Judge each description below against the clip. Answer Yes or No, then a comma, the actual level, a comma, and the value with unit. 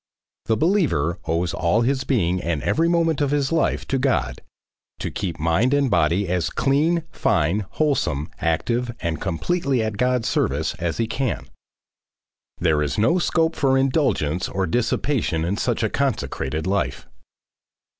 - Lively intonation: Yes, wide, 8.7 semitones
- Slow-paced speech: No, average, 150 wpm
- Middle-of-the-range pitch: No, low, 110 Hz